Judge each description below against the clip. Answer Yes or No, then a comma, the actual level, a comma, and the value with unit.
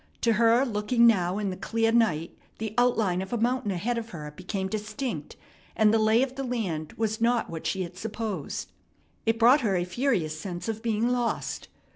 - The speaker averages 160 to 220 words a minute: Yes, average, 195 wpm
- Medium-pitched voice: No, high, 220 Hz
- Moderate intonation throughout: Yes, average, 3.9 semitones